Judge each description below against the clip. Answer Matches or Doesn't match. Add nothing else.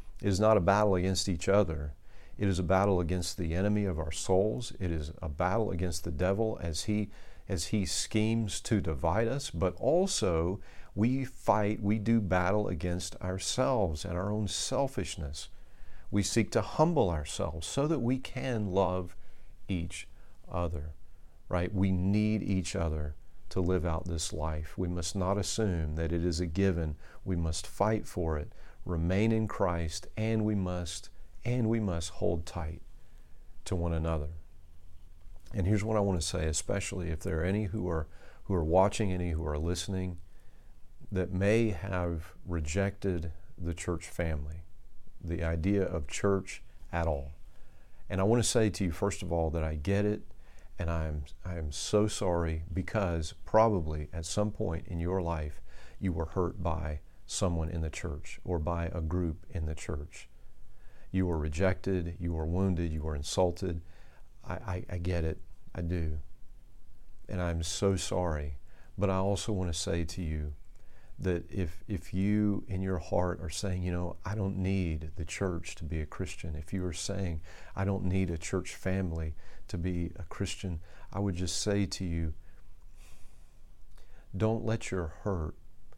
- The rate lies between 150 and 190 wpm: Matches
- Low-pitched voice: Matches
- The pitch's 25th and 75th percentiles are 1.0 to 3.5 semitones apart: Matches